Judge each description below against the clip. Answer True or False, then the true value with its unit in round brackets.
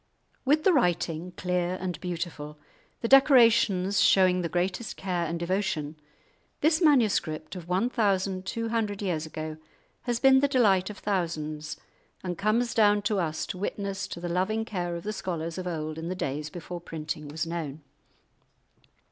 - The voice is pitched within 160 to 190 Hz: True (185 Hz)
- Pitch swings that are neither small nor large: True (4.1 semitones)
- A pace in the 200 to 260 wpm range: False (165 wpm)